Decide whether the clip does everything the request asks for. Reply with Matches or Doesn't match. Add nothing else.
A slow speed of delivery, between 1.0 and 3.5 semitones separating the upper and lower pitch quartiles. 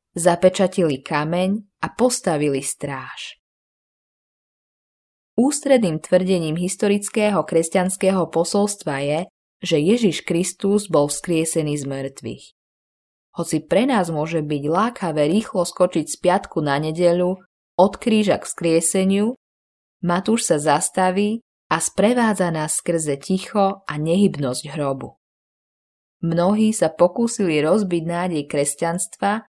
Doesn't match